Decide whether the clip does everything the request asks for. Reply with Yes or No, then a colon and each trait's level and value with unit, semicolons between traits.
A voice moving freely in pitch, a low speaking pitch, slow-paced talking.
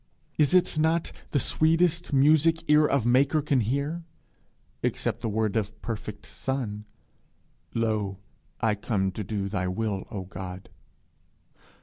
Yes: wide, 6.6 semitones; low, 115 Hz; slow, 130 wpm